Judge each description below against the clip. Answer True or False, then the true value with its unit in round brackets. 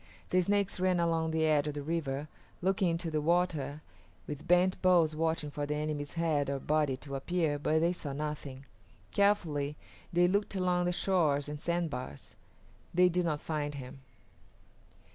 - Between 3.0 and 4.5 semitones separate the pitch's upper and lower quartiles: True (3.3 semitones)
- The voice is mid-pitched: True (160 Hz)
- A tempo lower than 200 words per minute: True (165 wpm)